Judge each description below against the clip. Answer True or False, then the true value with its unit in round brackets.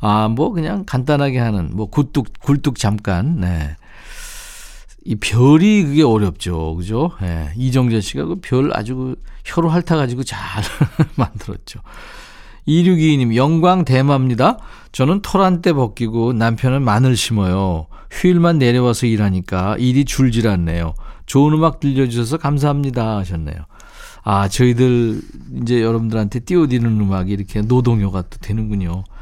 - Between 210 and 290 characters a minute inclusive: False (300 characters per minute)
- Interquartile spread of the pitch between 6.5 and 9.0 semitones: False (5.8 semitones)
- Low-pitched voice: True (120 Hz)